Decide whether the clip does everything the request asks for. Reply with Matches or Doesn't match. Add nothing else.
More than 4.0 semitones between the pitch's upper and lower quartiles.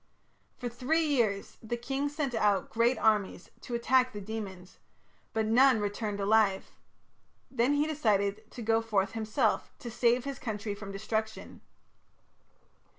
Doesn't match